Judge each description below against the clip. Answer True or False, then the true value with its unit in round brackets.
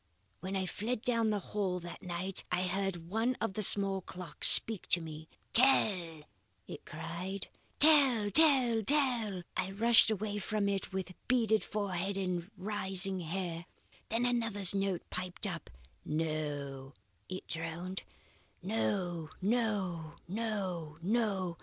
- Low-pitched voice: False (190 Hz)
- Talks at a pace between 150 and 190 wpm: False (135 wpm)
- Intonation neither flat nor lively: True (3.8 semitones)